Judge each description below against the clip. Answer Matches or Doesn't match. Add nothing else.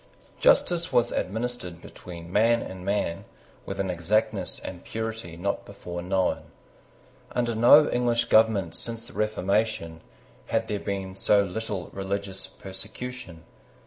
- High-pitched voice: Doesn't match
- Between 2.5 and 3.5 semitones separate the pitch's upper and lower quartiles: Doesn't match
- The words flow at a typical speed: Doesn't match